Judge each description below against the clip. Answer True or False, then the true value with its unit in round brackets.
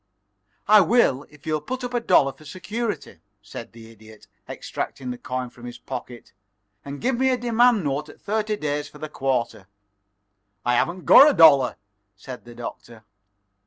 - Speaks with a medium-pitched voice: True (145 Hz)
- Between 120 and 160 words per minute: False (170 wpm)